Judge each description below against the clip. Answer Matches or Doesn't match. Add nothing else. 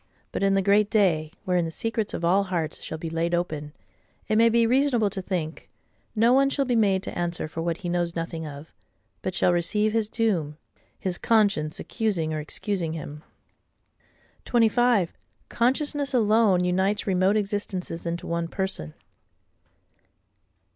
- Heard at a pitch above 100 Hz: Matches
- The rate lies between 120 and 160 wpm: Matches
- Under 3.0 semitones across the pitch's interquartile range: Doesn't match